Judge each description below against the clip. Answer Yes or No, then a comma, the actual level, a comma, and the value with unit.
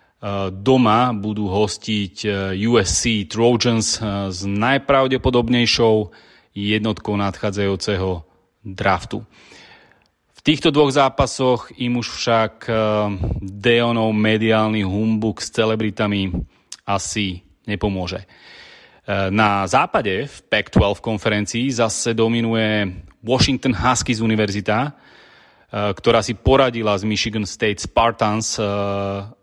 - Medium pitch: No, low, 110 Hz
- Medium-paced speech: No, slow, 85 wpm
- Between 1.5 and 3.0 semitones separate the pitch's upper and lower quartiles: Yes, average, 2.7 semitones